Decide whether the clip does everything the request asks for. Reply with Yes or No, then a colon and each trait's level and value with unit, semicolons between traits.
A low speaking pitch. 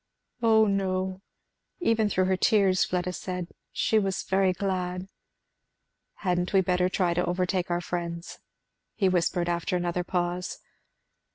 No: medium, 185 Hz